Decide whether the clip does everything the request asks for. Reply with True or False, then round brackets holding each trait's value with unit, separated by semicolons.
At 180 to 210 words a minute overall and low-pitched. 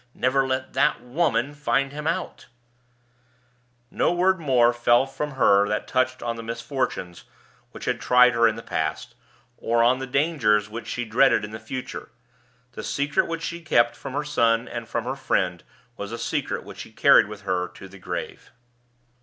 True (185 wpm; 125 Hz)